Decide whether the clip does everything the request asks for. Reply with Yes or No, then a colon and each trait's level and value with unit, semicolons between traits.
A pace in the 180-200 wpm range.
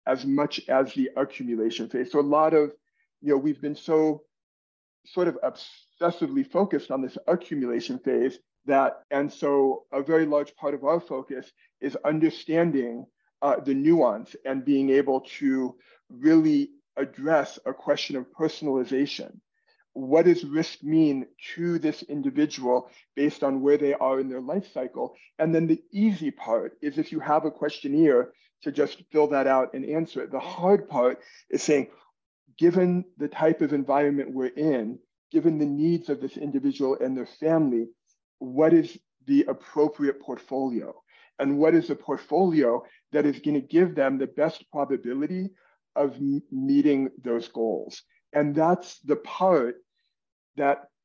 No: average, 155 wpm